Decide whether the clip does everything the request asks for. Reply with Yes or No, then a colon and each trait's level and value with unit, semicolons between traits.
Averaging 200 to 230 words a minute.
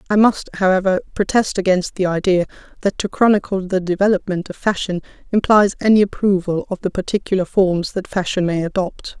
No: average, 165 wpm